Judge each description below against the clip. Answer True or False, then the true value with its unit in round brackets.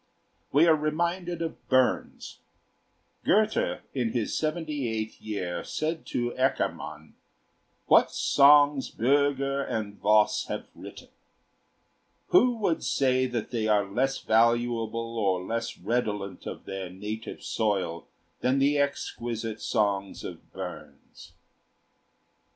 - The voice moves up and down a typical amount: True (4.8 semitones)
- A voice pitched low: True (120 Hz)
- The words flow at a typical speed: False (110 wpm)